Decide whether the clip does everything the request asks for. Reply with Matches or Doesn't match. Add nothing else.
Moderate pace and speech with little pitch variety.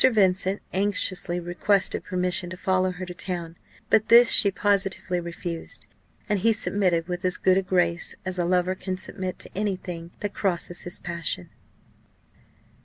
Matches